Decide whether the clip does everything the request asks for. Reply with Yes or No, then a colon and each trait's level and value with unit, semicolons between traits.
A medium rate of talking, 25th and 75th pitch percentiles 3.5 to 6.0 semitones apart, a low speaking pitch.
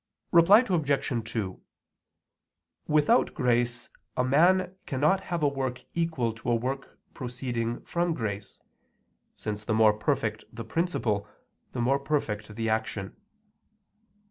No: slow, 120 wpm; average, 5.3 semitones; low, 125 Hz